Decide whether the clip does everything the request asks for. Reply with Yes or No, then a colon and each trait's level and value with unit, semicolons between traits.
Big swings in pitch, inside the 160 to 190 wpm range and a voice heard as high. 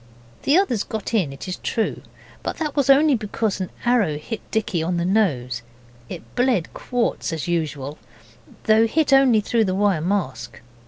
Yes: wide, 6.7 semitones; average, 175 wpm; high, 205 Hz